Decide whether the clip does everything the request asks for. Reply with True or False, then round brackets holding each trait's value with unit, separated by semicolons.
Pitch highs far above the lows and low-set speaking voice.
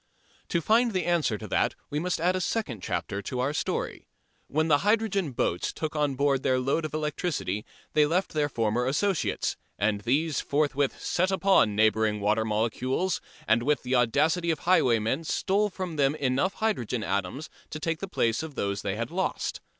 False (6.9 semitones; 145 Hz)